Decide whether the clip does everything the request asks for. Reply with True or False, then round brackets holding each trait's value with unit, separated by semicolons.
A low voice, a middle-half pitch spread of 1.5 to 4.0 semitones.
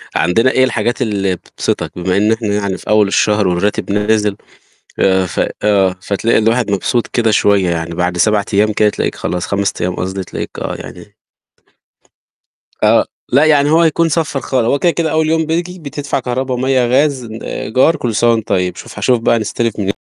False (110 Hz; 4.8 semitones)